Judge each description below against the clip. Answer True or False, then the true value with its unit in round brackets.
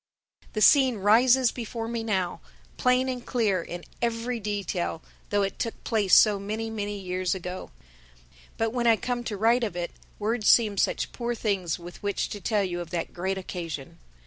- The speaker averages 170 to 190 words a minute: True (180 wpm)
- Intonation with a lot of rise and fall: False (4.0 semitones)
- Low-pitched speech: False (210 Hz)